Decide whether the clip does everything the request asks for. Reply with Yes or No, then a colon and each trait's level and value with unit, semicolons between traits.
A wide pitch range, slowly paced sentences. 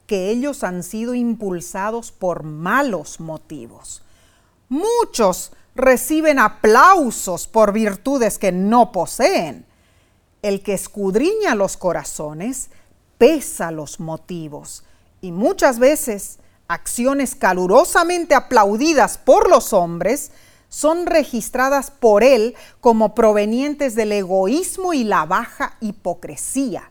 Yes: wide, 7.0 semitones; slow, 100 wpm